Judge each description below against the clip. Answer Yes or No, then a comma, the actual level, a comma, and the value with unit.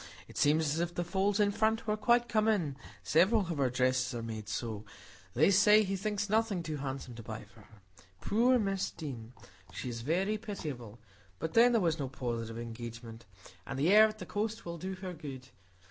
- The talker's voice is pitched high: No, medium, 165 Hz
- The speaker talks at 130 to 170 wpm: No, average, 200 wpm